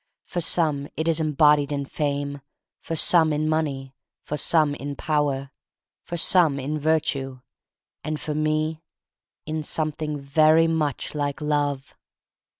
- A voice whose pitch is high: No, medium, 150 Hz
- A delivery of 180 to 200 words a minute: No, average, 145 wpm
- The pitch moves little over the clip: Yes, narrow, 1.8 semitones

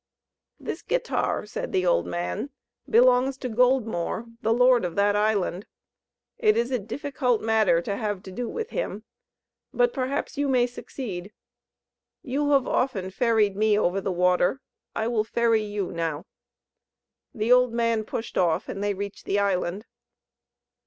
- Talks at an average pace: Yes, average, 150 wpm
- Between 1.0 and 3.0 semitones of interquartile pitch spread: No, average, 4.4 semitones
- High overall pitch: Yes, high, 220 Hz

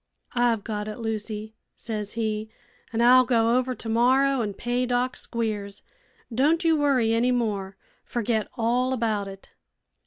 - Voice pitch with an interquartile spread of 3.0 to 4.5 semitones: No, narrow, 2.6 semitones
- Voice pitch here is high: Yes, high, 230 Hz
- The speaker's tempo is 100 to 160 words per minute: Yes, average, 145 wpm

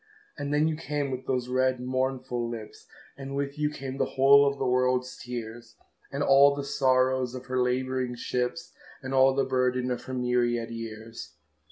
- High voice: No, low, 130 Hz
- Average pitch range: No, narrow, 1.7 semitones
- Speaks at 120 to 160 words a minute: No, average, 180 wpm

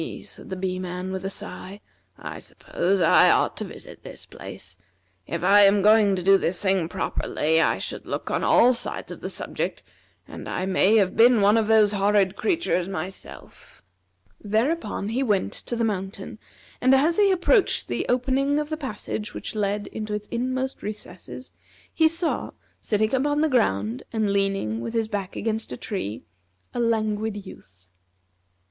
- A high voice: Yes, high, 210 Hz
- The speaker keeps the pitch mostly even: No, average, 4.1 semitones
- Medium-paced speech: Yes, average, 170 wpm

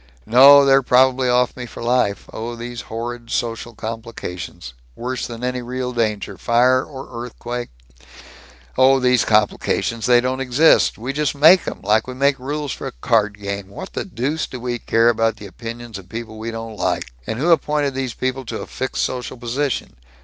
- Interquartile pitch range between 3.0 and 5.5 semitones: No, narrow, 2.4 semitones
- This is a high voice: No, low, 120 Hz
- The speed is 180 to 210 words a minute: Yes, average, 185 wpm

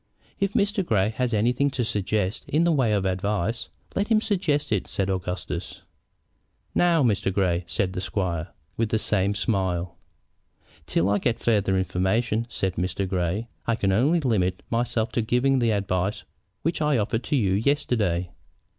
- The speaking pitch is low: Yes, low, 105 Hz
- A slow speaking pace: No, average, 165 wpm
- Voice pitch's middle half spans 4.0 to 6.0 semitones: Yes, average, 4.7 semitones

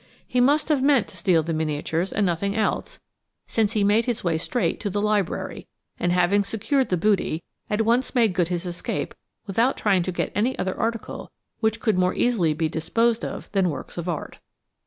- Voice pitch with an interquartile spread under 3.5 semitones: No, average, 4.6 semitones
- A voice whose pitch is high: Yes, high, 200 Hz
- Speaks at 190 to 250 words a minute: Yes, average, 200 wpm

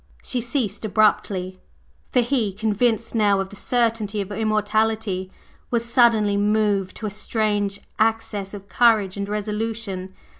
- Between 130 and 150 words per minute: Yes, average, 140 wpm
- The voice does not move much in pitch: Yes, narrow, 2.0 semitones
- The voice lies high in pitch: Yes, high, 210 Hz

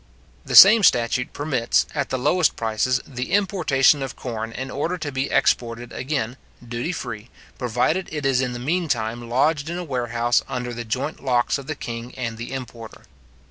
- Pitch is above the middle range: No, low, 130 Hz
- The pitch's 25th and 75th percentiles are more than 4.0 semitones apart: No, average, 3.7 semitones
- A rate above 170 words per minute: Yes, average, 180 wpm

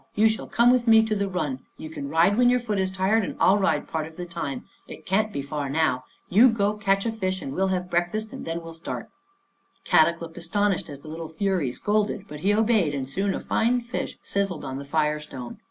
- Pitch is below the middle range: No, medium, 185 Hz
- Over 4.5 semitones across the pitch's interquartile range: Yes, average, 5.0 semitones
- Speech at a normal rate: No, fast, 235 wpm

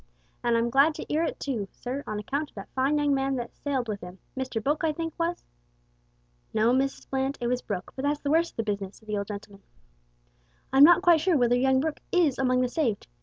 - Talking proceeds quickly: Yes, fast, 240 wpm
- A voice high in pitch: Yes, very high, 260 Hz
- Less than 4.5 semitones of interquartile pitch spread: No, average, 5.1 semitones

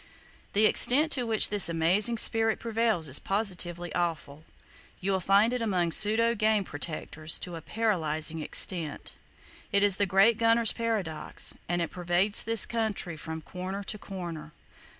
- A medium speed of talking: Yes, average, 150 wpm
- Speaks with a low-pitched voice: No, high, 195 Hz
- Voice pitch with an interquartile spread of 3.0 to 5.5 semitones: Yes, average, 4.8 semitones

